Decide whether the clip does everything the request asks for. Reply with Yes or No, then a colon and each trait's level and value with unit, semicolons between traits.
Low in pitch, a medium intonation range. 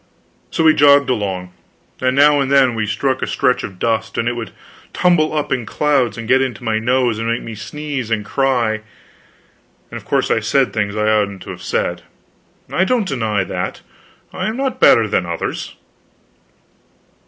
Yes: low, 120 Hz; average, 4.5 semitones